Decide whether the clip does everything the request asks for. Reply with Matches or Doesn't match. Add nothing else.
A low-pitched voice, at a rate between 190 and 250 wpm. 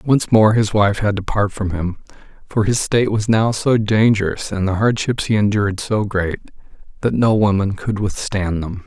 Matches